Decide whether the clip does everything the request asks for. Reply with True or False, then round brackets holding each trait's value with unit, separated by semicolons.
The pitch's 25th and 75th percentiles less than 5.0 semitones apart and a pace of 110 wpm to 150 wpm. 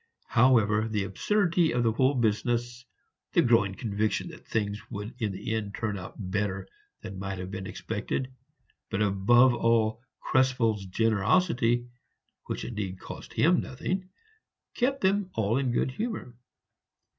True (4.0 semitones; 140 wpm)